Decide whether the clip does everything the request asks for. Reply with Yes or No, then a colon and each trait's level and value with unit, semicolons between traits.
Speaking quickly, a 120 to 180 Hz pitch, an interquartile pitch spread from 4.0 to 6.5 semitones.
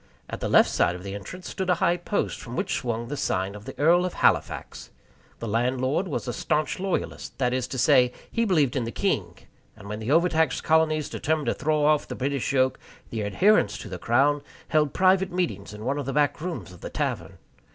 Yes: fast, 220 wpm; medium, 140 Hz; wide, 5.6 semitones